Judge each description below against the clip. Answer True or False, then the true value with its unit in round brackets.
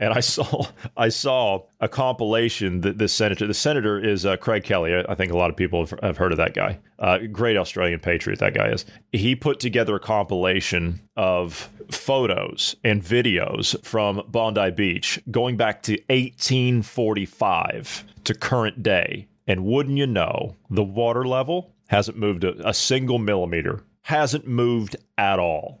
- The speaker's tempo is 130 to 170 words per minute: True (165 wpm)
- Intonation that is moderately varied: True (4.0 semitones)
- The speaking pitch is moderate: False (105 Hz)